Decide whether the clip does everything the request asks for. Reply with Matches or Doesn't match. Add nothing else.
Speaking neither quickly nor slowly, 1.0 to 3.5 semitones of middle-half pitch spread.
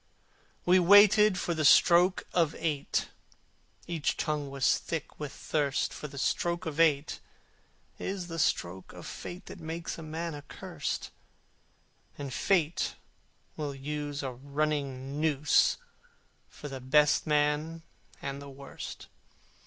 Doesn't match